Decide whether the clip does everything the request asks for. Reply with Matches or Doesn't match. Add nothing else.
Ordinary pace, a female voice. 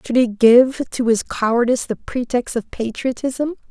Matches